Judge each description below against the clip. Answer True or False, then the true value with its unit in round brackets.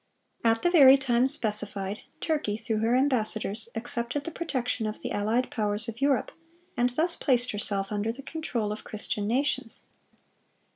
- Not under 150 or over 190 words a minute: True (160 wpm)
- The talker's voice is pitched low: False (235 Hz)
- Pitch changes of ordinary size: True (3.9 semitones)